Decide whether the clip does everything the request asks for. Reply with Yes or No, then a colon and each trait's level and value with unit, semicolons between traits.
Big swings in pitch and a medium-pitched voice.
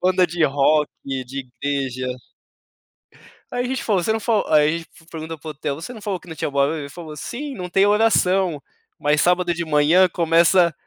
No: average, 3.9 semitones; medium, 165 Hz